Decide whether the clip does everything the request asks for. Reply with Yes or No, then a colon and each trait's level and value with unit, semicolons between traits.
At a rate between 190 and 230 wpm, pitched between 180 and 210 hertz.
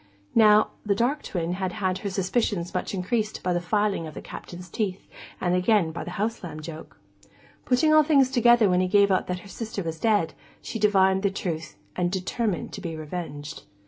Yes: average, 200 wpm; high, 190 Hz